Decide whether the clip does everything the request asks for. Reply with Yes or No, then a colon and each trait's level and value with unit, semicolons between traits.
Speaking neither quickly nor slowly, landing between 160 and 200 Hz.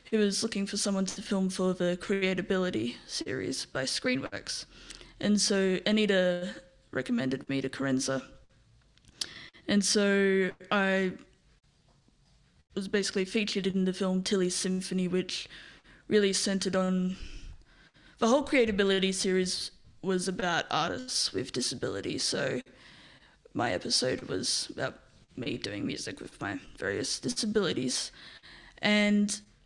No: slow, 115 wpm; high, 190 Hz